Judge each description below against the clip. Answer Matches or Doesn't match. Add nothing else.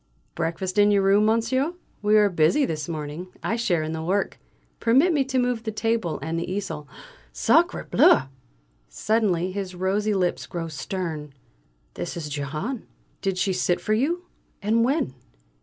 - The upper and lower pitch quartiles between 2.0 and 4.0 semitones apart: Doesn't match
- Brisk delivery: Doesn't match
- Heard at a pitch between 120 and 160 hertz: Doesn't match